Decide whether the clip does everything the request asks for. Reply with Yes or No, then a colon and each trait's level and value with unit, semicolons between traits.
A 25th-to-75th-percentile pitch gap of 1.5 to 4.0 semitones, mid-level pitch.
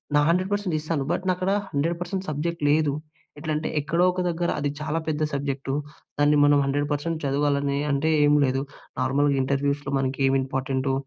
Yes: average, 2.8 semitones; medium, 145 Hz